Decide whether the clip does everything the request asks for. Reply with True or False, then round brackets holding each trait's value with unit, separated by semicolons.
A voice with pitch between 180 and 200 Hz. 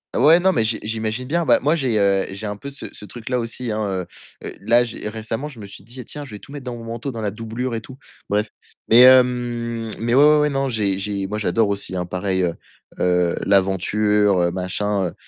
False (110 Hz)